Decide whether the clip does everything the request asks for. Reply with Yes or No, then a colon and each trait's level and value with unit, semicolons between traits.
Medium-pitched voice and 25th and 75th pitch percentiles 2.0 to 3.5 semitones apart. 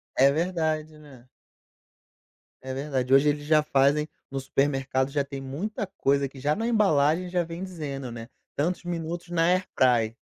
No: medium, 150 Hz; average, 3.9 semitones